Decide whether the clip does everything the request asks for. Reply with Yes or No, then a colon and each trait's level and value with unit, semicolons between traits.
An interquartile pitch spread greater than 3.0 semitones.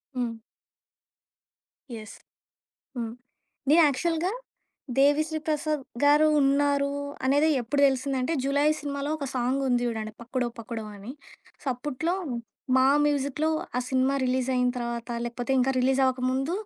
No: narrow, 2.6 semitones